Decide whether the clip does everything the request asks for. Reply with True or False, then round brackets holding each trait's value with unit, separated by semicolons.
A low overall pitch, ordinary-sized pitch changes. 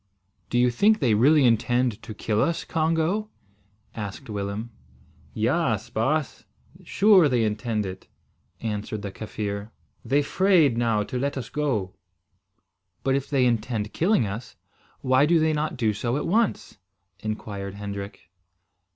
False (120 Hz; 5.9 semitones)